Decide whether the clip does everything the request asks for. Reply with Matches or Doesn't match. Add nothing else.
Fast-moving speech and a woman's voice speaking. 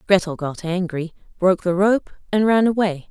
Doesn't match